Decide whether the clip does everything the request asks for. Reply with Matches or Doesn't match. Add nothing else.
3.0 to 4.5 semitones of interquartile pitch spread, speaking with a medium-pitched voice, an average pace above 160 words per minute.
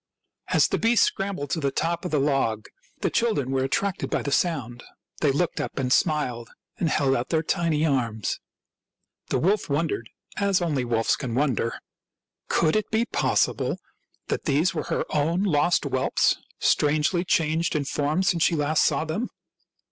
Matches